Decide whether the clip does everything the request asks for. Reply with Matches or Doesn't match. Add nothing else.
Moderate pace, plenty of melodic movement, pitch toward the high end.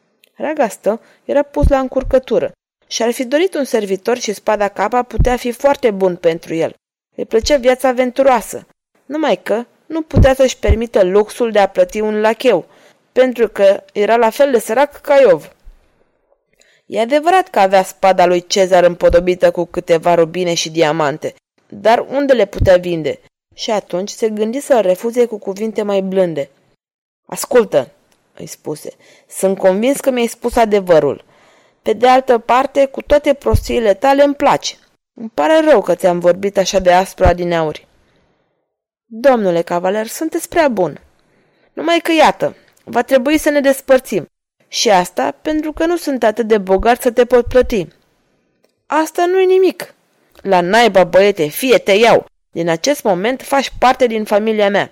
Matches